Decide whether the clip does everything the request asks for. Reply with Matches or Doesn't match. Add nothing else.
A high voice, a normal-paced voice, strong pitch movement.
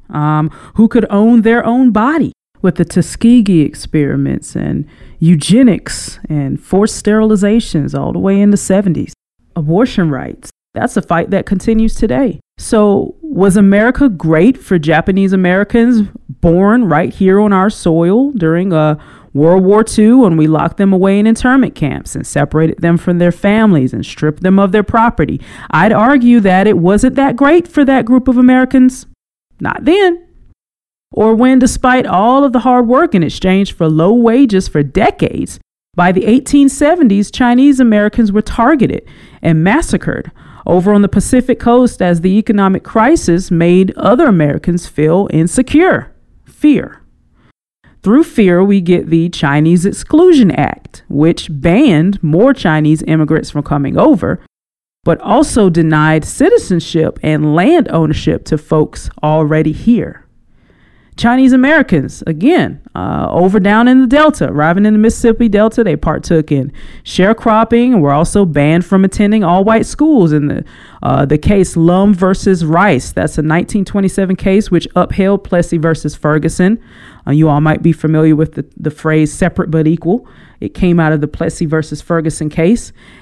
Matches